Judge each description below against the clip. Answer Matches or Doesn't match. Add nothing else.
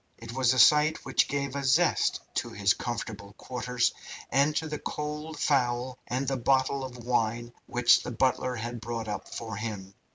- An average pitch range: Matches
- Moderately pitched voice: Doesn't match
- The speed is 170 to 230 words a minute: Matches